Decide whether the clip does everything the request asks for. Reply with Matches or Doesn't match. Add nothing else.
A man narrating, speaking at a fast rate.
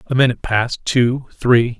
Doesn't match